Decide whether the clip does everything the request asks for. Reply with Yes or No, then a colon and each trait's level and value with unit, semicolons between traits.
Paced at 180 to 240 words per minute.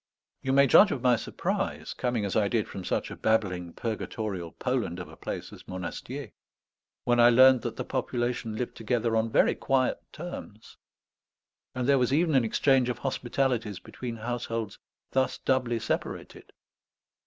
No: average, 160 wpm